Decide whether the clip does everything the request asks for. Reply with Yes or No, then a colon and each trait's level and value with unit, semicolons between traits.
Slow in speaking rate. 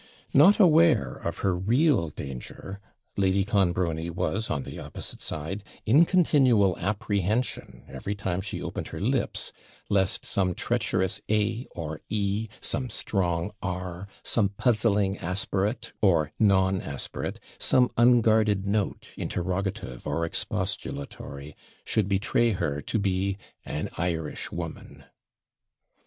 Yes: slow, 115 wpm